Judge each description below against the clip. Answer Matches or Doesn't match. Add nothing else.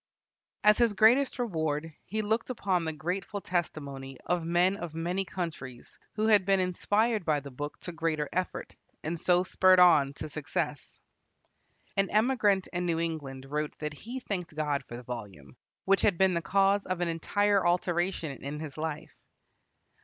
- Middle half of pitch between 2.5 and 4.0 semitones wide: Doesn't match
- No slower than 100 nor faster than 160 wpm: Doesn't match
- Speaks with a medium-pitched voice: Matches